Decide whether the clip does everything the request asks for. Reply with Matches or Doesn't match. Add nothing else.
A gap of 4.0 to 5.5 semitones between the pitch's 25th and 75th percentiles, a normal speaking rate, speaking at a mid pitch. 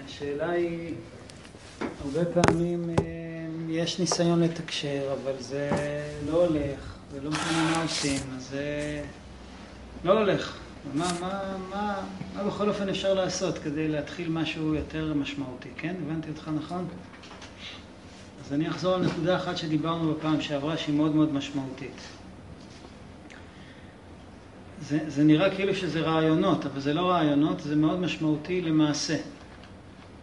Doesn't match